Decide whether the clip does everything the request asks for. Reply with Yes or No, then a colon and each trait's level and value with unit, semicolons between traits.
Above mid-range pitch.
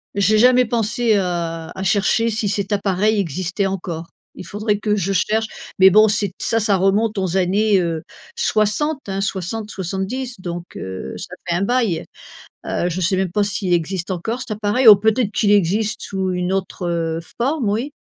Yes: high, 200 Hz